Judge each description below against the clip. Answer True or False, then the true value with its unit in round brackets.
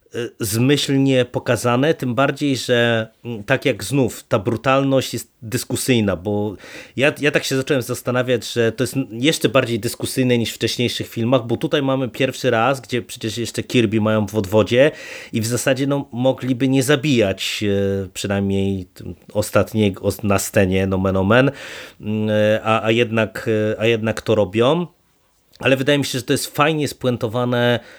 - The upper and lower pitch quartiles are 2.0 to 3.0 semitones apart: False (3.4 semitones)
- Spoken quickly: False (150 wpm)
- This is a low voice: True (120 Hz)